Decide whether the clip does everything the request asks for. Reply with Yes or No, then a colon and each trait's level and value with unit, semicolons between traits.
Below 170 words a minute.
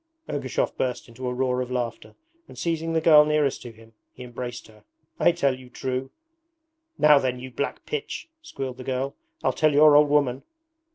No: average, 185 wpm